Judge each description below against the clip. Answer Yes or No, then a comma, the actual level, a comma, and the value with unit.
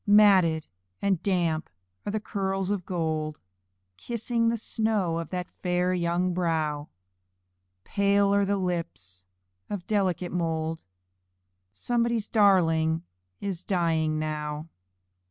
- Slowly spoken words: Yes, slow, 110 wpm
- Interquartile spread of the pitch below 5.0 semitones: Yes, average, 3.9 semitones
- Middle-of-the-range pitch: Yes, medium, 180 Hz